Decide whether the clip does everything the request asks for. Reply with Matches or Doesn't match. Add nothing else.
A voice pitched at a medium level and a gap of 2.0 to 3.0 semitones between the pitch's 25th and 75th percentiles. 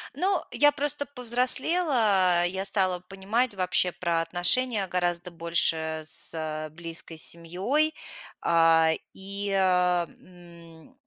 Doesn't match